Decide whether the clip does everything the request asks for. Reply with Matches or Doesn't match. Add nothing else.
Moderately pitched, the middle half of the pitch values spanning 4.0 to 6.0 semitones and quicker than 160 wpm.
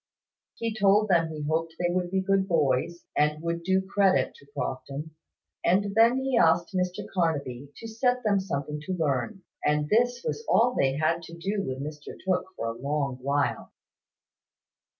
Matches